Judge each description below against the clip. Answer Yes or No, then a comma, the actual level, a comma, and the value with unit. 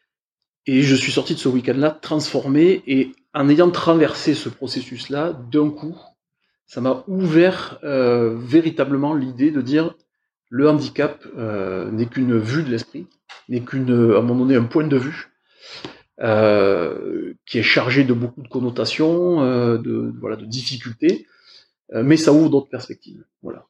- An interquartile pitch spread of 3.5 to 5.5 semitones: Yes, average, 3.8 semitones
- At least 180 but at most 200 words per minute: No, average, 155 wpm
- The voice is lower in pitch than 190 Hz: Yes, low, 135 Hz